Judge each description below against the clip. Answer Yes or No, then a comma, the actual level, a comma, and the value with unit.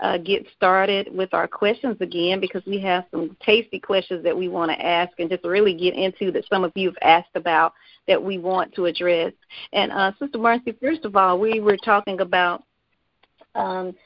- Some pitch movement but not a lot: No, narrow, 2.1 semitones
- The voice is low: No, high, 190 Hz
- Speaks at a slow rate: No, average, 200 wpm